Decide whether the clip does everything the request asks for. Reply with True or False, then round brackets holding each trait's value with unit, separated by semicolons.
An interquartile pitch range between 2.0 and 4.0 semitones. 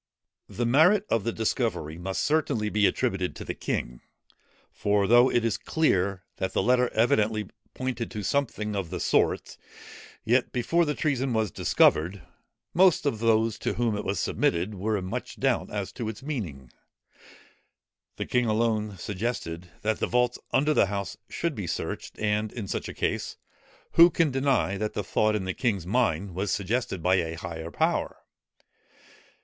False (4.4 semitones)